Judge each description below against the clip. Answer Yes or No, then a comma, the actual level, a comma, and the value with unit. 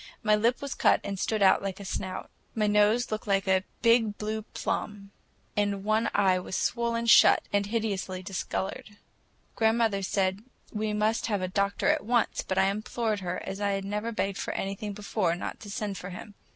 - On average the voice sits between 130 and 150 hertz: No, high, 205 Hz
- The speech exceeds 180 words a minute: Yes, average, 190 wpm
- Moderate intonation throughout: No, narrow, 2.0 semitones